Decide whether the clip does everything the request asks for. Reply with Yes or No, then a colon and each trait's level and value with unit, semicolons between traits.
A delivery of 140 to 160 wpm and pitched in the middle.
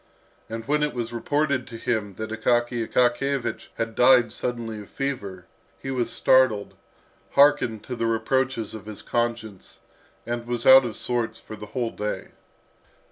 No: average, 155 wpm; low, 120 Hz